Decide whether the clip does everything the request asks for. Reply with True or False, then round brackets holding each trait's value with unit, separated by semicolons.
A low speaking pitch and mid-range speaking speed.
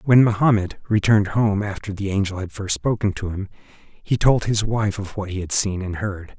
False (100 Hz; 215 wpm)